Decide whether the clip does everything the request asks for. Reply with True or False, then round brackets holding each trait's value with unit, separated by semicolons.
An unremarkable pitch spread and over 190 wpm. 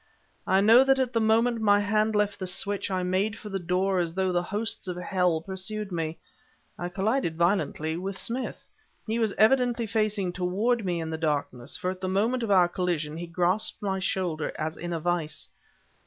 True (3.5 semitones; 200 wpm)